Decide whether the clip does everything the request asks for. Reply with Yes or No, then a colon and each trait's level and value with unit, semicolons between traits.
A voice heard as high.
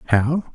No: low, 135 Hz